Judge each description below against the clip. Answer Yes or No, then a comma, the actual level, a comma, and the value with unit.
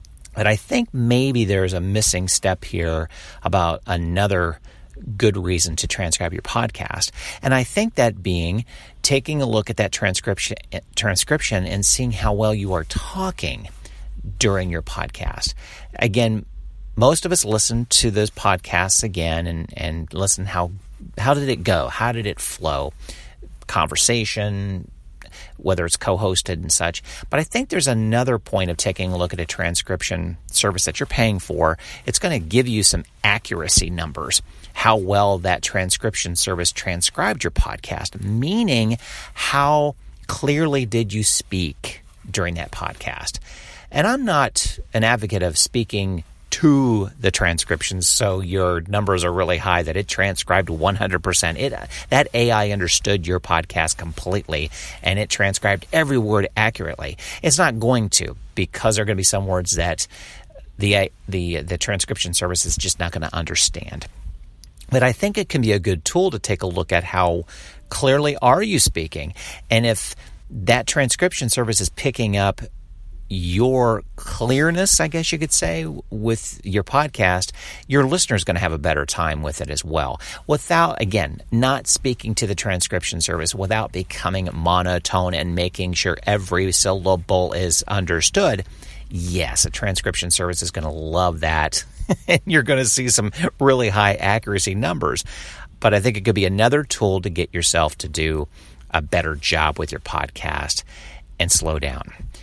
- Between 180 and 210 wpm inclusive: No, average, 160 wpm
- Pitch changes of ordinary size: Yes, average, 4.7 semitones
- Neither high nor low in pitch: No, very low, 95 Hz